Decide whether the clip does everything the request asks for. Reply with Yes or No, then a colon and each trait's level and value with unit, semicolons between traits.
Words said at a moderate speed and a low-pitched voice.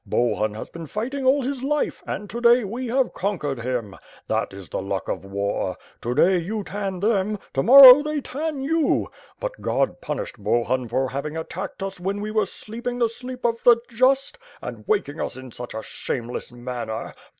No: average, 190 wpm; high, 205 Hz